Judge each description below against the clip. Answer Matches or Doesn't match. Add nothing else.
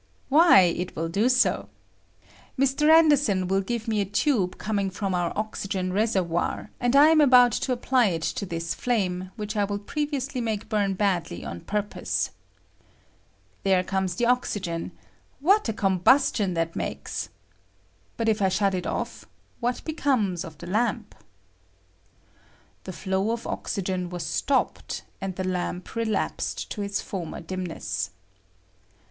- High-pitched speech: Matches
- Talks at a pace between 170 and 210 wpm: Doesn't match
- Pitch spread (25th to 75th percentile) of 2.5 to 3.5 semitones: Doesn't match